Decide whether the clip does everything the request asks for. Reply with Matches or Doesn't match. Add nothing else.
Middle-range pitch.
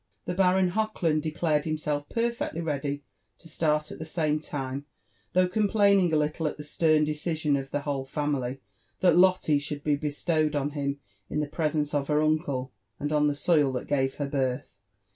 Matches